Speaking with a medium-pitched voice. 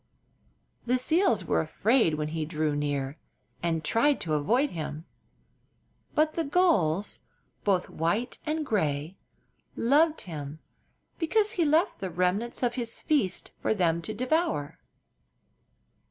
No: high, 205 Hz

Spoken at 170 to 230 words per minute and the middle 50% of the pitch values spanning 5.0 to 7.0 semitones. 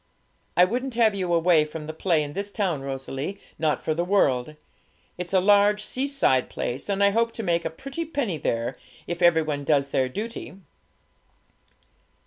Yes: average, 175 wpm; average, 5.3 semitones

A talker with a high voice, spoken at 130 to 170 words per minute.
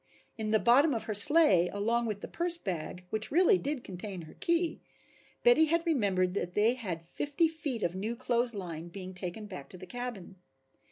No: high, 220 Hz; average, 190 wpm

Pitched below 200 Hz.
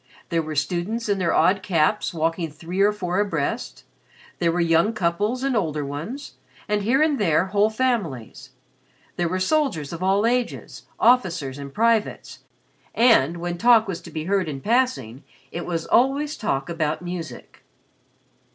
Yes: medium, 185 Hz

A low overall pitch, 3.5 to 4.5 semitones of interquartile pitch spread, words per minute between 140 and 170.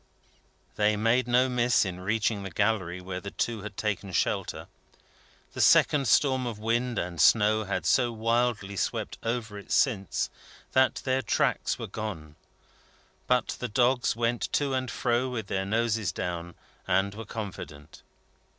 Yes: low, 110 Hz; average, 3.8 semitones; average, 150 wpm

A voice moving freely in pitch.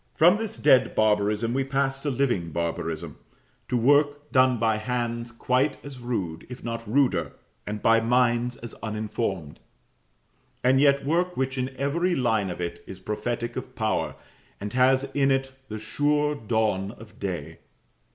No: average, 4.2 semitones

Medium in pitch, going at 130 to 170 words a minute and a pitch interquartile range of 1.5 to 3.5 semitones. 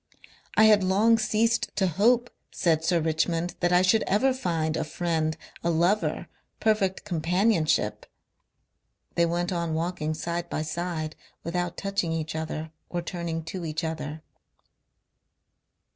Yes: medium, 170 Hz; slow, 135 wpm; average, 3.2 semitones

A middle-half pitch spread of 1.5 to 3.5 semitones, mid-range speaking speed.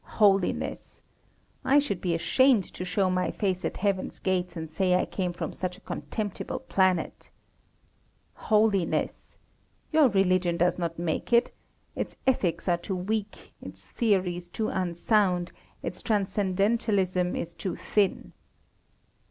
No: average, 2.8 semitones; slow, 130 wpm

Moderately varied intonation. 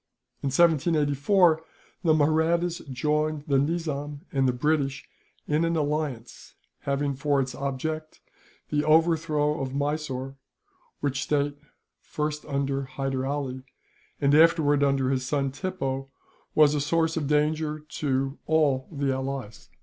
No: narrow, 2.3 semitones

